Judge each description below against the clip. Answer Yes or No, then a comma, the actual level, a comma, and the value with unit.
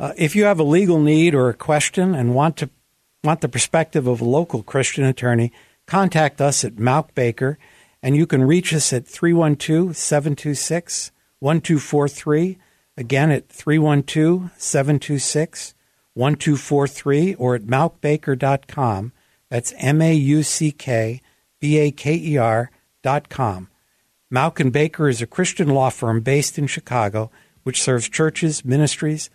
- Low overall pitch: No, medium, 145 Hz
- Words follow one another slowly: Yes, slow, 130 wpm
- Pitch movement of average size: Yes, average, 3.3 semitones